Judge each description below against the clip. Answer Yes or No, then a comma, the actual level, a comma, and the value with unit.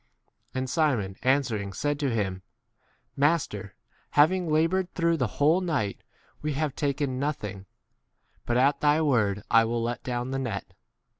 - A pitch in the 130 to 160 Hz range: Yes, low, 135 Hz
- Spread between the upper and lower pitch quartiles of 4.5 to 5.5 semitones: Yes, average, 5.1 semitones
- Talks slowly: No, average, 150 wpm